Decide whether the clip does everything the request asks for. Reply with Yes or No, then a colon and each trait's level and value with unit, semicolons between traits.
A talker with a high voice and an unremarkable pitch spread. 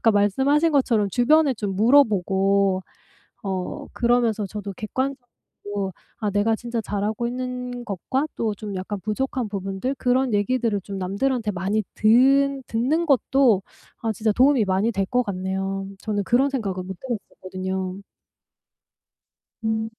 Yes: high, 220 Hz; average, 4.2 semitones